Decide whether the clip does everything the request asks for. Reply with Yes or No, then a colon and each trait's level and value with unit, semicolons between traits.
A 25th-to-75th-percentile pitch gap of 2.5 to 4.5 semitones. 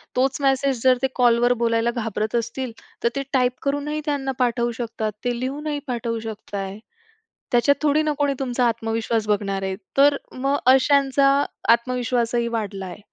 Yes: average, 3.0 semitones